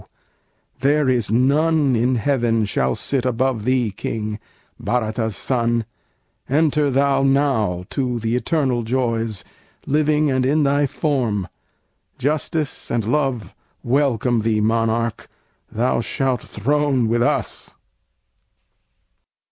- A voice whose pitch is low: Yes, low, 125 Hz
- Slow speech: Yes, slow, 110 wpm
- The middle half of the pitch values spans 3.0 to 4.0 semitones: Yes, average, 3.7 semitones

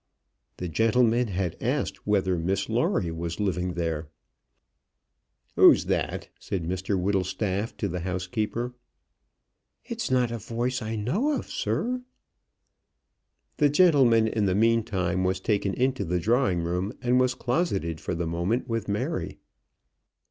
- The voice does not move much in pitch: No, average, 4.9 semitones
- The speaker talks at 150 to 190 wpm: No, slow, 135 wpm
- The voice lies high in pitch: No, low, 105 Hz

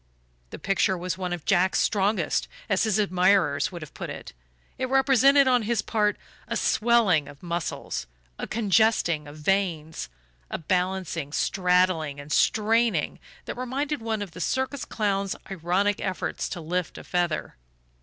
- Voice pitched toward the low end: No, high, 190 Hz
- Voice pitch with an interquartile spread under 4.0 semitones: No, average, 4.3 semitones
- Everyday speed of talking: Yes, average, 150 wpm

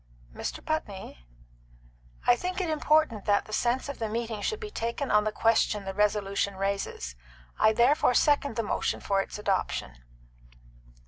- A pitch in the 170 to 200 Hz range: No, high, 220 Hz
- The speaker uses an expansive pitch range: Yes, wide, 5.8 semitones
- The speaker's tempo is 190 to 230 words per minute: No, average, 155 wpm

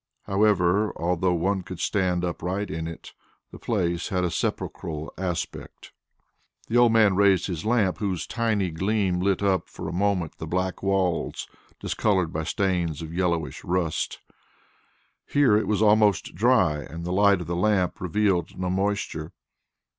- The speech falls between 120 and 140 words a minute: No, average, 155 wpm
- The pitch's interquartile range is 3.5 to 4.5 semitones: No, average, 2.8 semitones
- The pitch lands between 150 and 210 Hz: No, very low, 95 Hz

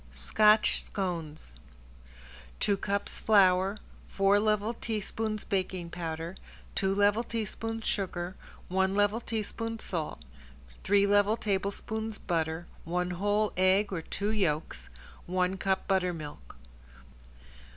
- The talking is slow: Yes, slow, 105 wpm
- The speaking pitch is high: Yes, high, 195 Hz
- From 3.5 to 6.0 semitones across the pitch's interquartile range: No, average, 2.9 semitones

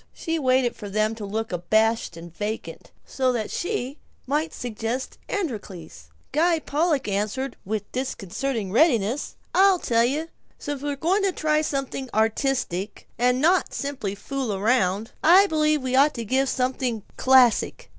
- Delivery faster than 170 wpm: No, average, 155 wpm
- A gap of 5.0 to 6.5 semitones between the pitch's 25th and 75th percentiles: Yes, wide, 5.4 semitones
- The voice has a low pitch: No, very high, 255 Hz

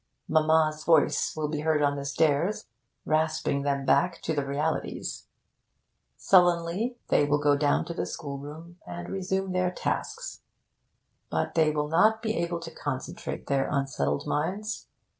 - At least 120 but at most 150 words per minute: Yes, average, 145 wpm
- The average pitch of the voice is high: No, medium, 155 Hz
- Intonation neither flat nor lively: Yes, average, 3.3 semitones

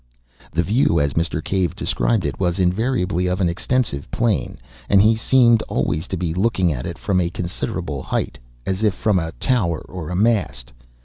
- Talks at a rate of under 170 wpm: No, average, 185 wpm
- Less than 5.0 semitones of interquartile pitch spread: Yes, average, 4.5 semitones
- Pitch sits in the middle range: No, very low, 90 Hz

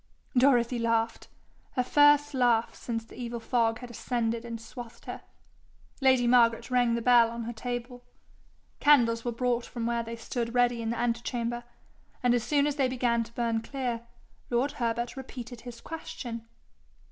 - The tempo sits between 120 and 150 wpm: No, average, 170 wpm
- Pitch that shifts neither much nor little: No, narrow, 1.2 semitones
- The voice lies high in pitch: Yes, high, 240 Hz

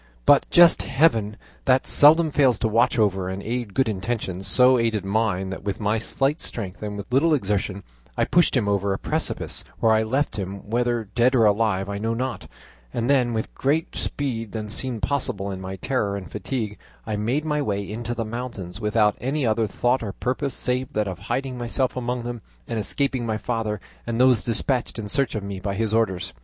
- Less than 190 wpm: No, average, 200 wpm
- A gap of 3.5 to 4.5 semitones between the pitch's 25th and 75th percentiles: Yes, average, 3.9 semitones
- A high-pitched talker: No, low, 115 Hz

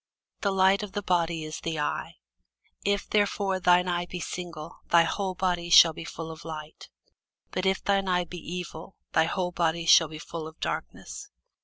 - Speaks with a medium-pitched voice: Yes, medium, 175 Hz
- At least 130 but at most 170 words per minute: No, average, 185 wpm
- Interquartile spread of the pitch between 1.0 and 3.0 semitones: Yes, narrow, 2.6 semitones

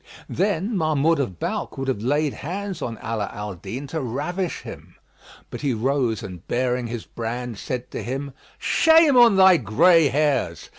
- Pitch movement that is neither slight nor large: No, wide, 6.3 semitones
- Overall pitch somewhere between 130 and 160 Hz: Yes, low, 135 Hz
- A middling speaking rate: Yes, average, 170 wpm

